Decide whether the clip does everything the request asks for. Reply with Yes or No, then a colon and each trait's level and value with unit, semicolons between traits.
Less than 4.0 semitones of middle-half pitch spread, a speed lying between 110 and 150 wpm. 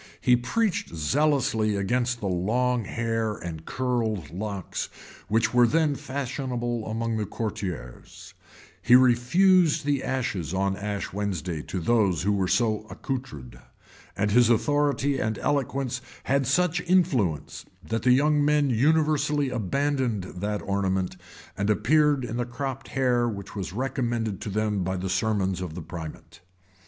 No: average, 5.2 semitones; average, 140 wpm